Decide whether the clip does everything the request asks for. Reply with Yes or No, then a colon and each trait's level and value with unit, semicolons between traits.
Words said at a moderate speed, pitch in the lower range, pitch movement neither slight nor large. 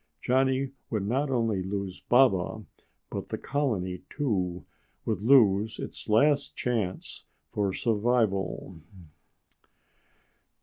No: slow, 95 wpm; low, 110 Hz; average, 5.0 semitones